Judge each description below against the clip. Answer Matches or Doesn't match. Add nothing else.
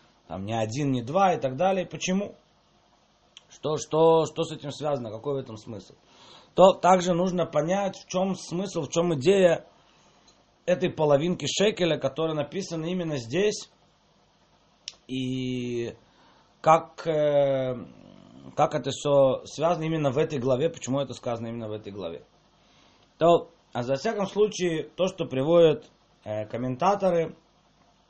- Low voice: Doesn't match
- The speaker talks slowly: Doesn't match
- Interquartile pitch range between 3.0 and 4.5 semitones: Doesn't match